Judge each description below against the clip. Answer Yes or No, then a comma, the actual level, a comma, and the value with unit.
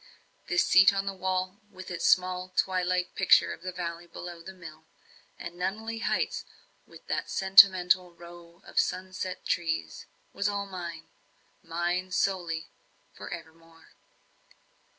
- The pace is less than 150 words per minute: Yes, slow, 135 wpm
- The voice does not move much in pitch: Yes, narrow, 1.8 semitones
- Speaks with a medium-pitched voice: Yes, medium, 180 Hz